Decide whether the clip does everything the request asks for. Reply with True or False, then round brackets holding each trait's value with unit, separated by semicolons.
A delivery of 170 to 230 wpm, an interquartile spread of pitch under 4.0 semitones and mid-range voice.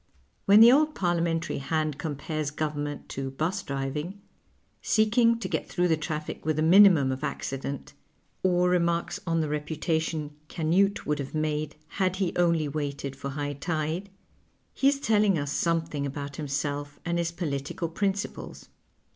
False (155 wpm; 3.6 semitones; 160 Hz)